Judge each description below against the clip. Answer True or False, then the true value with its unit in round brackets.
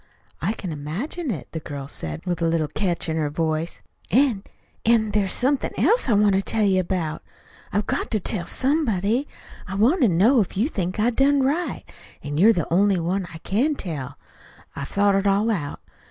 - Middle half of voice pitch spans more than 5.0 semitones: True (5.6 semitones)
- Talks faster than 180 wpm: True (200 wpm)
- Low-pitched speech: False (195 Hz)